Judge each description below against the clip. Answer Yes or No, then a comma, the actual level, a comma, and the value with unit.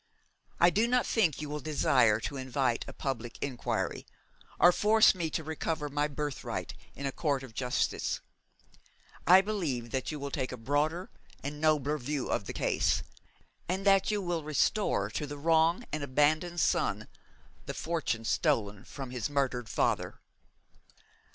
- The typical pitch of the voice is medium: Yes, medium, 145 Hz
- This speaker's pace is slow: No, average, 155 wpm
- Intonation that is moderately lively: Yes, average, 4.3 semitones